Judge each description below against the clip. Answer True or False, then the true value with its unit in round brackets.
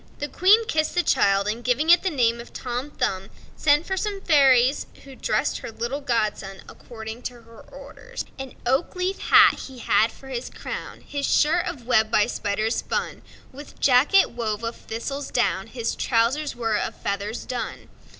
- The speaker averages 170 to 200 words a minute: True (185 wpm)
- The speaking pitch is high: True (250 Hz)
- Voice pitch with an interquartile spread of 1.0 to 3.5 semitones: False (4.3 semitones)